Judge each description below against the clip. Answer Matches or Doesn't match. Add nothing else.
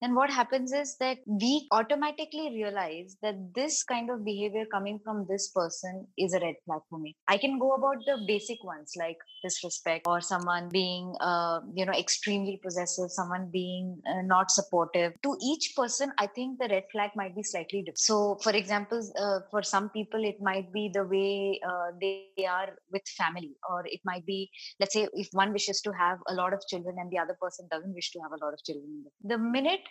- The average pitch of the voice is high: Matches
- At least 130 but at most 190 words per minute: Doesn't match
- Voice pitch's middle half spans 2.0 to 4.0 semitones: Matches